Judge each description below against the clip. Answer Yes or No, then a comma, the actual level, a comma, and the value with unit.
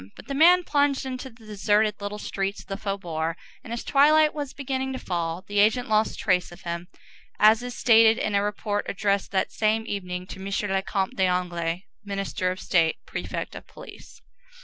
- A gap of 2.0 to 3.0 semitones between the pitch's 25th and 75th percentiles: No, average, 3.8 semitones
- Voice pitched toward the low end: No, high, 205 Hz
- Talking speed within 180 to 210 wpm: Yes, average, 190 wpm